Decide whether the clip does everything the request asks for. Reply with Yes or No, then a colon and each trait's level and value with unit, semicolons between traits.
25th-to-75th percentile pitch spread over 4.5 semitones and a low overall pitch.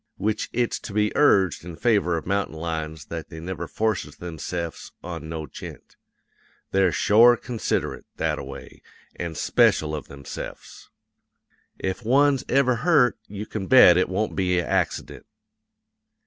Yes: average, 5.2 semitones; very low, 95 Hz